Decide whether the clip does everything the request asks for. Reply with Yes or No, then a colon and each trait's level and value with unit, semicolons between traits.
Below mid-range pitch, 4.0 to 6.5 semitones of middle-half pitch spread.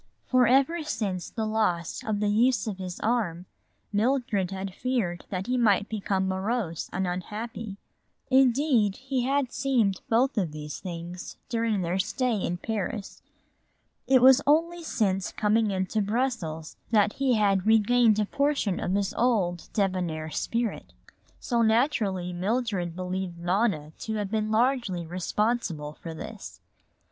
No: high, 210 Hz; average, 4.6 semitones